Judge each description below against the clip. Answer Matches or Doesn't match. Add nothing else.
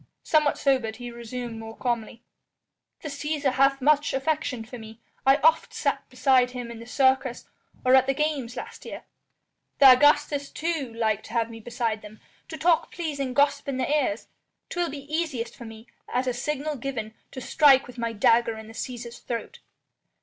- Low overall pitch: Doesn't match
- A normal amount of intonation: Matches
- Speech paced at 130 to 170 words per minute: Doesn't match